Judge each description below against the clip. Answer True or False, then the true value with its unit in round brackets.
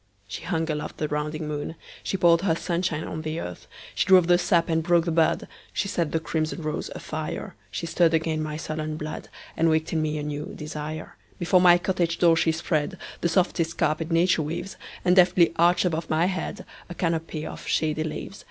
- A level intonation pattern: True (1.8 semitones)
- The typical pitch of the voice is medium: True (165 Hz)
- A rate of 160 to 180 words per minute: True (170 wpm)